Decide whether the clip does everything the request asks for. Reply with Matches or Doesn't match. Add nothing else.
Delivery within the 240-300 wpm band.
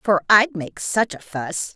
Doesn't match